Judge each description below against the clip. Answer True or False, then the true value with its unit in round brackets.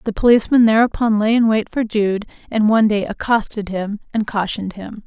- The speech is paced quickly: False (190 wpm)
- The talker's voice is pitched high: True (215 Hz)